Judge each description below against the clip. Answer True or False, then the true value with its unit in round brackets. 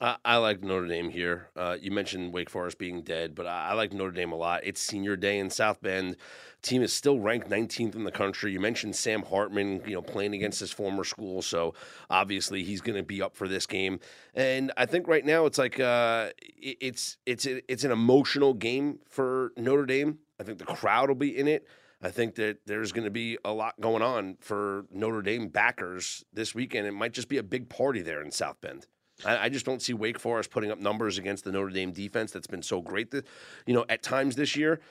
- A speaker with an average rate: False (225 wpm)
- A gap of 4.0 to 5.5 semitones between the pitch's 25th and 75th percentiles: True (4.8 semitones)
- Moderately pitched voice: False (110 Hz)